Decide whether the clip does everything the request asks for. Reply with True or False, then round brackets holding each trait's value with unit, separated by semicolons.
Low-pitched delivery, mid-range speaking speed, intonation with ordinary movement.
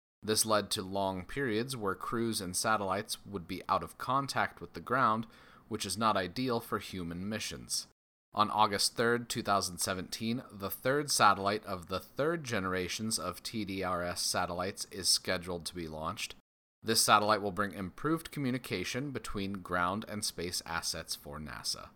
True (100 Hz; 155 wpm; 3.6 semitones)